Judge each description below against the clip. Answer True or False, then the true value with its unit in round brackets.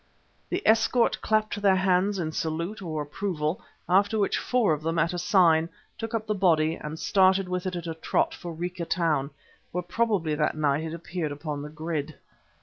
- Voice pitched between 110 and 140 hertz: False (170 Hz)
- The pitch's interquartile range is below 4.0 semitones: True (3.6 semitones)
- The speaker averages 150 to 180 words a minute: False (190 wpm)